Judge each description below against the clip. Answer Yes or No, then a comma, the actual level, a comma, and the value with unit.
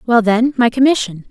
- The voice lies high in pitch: Yes, high, 235 Hz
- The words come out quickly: No, average, 140 wpm